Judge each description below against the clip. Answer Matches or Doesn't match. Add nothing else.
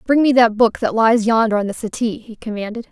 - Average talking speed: Doesn't match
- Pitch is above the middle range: Matches